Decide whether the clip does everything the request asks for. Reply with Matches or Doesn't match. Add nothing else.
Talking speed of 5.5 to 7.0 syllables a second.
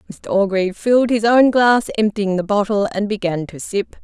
Doesn't match